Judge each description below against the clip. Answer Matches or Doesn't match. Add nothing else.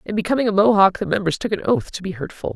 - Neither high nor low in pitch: Doesn't match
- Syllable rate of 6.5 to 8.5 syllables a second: Matches